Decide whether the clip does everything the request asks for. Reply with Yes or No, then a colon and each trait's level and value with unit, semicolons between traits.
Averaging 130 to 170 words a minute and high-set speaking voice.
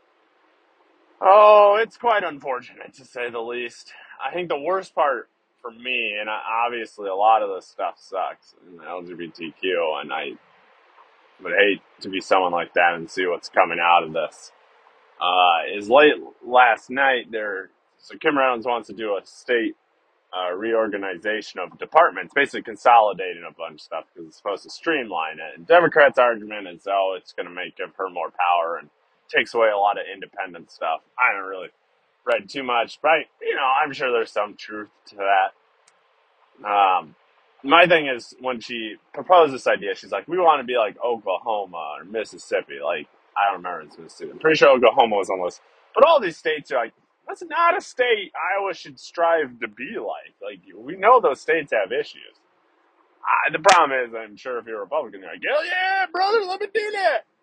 No: average, 190 wpm; high, 225 Hz